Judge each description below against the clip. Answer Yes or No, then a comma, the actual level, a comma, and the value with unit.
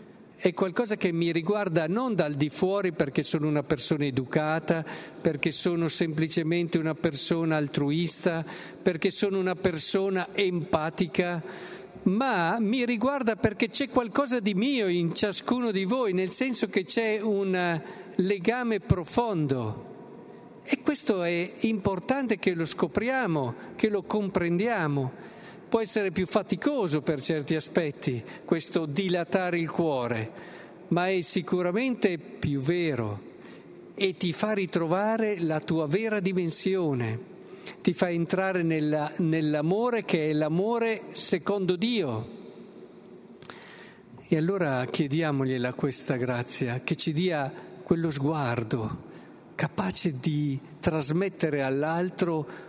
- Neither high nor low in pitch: Yes, medium, 180 Hz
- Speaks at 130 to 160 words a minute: No, slow, 115 wpm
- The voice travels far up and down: No, average, 4.3 semitones